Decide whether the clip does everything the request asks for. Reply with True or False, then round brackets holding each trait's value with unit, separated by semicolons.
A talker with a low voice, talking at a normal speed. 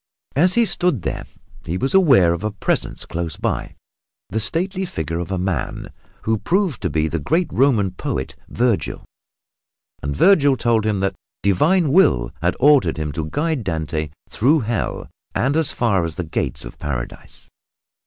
True (105 Hz; 165 wpm)